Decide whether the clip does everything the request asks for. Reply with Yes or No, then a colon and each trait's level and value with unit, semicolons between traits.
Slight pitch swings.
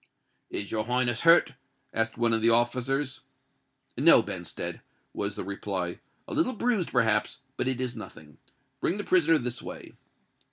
No: average, 4.6 semitones